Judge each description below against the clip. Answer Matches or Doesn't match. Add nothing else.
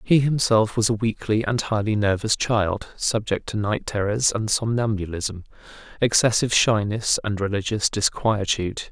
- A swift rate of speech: Doesn't match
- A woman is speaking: Doesn't match